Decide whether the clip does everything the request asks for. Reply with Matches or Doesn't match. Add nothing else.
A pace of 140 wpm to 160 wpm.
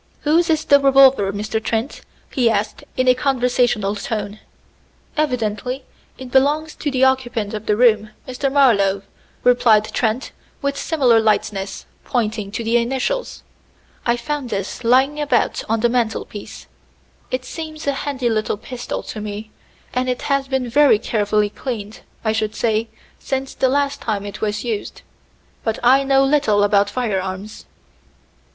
Matches